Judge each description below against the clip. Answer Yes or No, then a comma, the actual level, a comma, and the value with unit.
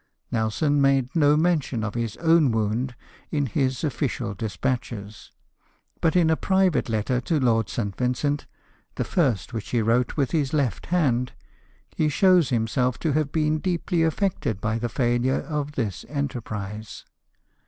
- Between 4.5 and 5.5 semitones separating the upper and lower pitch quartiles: Yes, average, 5.0 semitones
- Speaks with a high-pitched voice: No, low, 130 Hz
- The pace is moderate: Yes, average, 155 wpm